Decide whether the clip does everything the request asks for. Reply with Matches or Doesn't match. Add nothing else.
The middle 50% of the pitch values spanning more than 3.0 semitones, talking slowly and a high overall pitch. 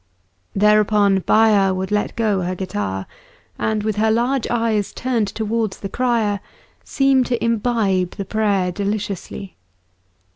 Doesn't match